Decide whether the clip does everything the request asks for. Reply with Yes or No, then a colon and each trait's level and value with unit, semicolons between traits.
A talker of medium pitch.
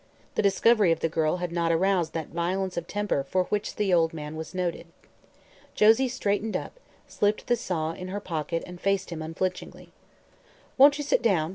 Yes: medium, 180 Hz